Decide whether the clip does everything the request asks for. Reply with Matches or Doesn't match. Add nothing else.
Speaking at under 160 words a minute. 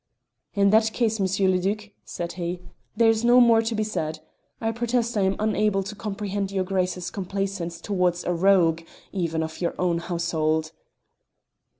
Doesn't match